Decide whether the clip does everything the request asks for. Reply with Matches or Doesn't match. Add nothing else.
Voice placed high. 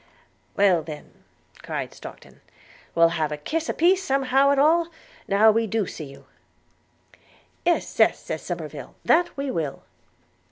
Matches